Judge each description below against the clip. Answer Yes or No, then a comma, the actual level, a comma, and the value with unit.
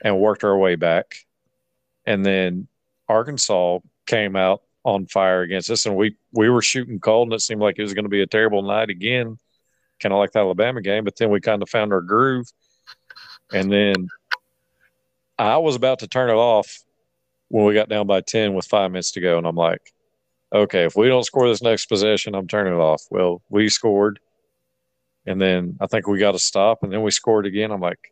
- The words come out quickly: Yes, fast, 215 wpm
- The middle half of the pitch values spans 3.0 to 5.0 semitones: No, narrow, 2.6 semitones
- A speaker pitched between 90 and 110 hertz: Yes, low, 105 Hz